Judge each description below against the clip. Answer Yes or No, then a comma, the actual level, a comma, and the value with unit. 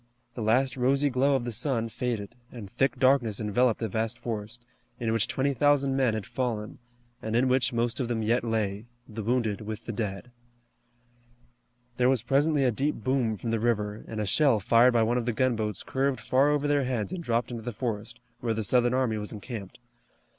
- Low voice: Yes, low, 120 Hz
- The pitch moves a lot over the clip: No, average, 2.8 semitones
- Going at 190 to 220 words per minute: Yes, fast, 205 wpm